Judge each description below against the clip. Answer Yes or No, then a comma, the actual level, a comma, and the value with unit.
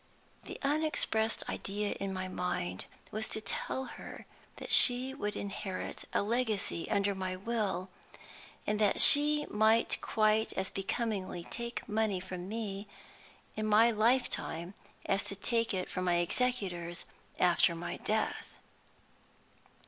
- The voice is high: Yes, high, 210 Hz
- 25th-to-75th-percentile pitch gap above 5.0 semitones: No, average, 3.5 semitones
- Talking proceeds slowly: Yes, slow, 130 wpm